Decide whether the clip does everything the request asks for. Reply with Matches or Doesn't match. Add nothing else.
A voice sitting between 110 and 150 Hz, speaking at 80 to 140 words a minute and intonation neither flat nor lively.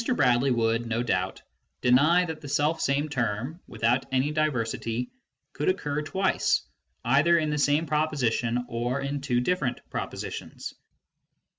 Matches